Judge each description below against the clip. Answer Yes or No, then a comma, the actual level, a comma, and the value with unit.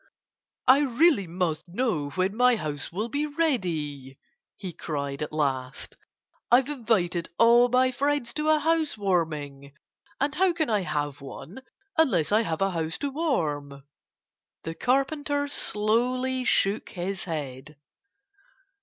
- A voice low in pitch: No, high, 205 Hz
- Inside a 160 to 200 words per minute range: No, slow, 135 wpm